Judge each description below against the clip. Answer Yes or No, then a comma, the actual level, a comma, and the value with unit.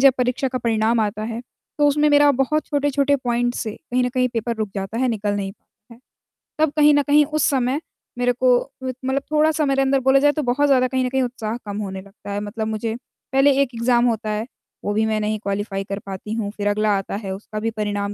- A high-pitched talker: Yes, high, 240 Hz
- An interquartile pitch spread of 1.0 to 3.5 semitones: No, average, 4.2 semitones